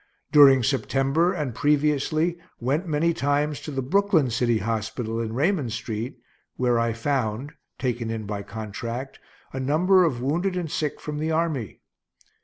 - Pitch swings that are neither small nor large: Yes, average, 4.9 semitones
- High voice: No, low, 135 Hz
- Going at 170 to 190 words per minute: No, average, 150 wpm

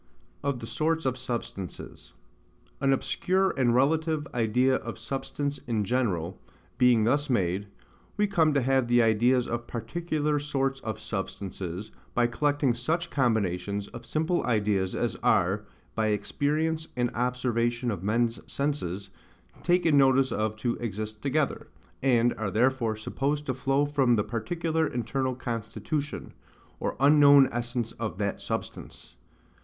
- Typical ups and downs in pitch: Yes, average, 4.5 semitones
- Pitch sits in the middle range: No, low, 125 Hz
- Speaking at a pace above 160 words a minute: No, slow, 135 wpm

